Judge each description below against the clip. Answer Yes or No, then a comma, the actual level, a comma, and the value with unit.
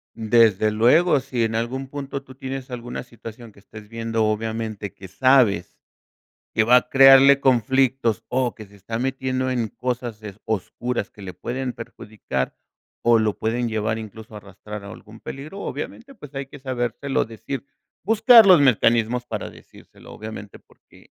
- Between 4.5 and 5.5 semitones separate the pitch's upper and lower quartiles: No, average, 3.4 semitones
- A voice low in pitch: Yes, low, 120 Hz